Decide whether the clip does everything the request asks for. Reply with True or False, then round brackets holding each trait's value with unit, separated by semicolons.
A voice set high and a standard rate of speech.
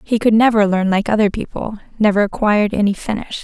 True (210 Hz; 190 wpm)